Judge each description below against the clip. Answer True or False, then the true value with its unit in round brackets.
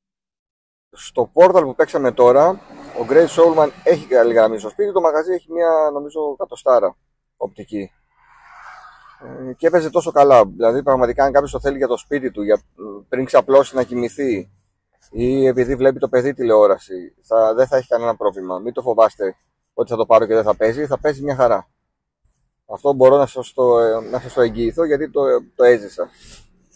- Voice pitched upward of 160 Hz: False (135 Hz)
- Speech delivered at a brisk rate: True (175 wpm)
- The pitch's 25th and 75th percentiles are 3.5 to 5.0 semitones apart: False (5.4 semitones)